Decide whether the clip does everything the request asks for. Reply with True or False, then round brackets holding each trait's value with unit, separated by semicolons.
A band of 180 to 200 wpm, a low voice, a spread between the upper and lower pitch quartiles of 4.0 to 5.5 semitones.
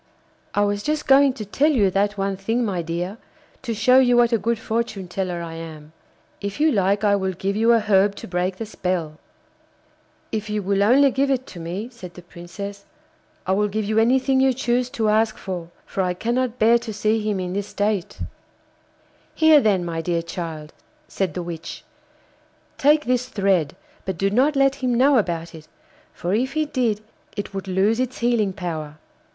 False (195 wpm; 205 Hz; 4.7 semitones)